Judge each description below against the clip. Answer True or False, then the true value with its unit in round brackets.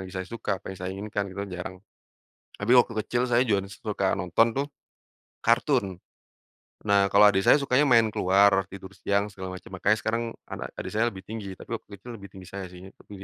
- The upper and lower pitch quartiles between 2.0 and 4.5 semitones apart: True (3.1 semitones)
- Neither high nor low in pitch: False (100 Hz)